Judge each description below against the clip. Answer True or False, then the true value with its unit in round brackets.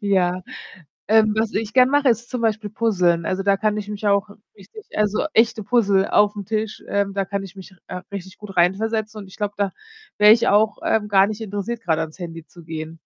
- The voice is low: False (205 Hz)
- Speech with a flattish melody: True (2.2 semitones)